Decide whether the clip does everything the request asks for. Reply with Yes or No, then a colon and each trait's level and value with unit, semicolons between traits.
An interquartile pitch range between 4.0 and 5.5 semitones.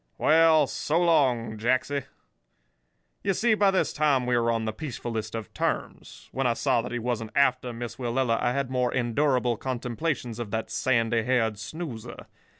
No: average, 3.4 semitones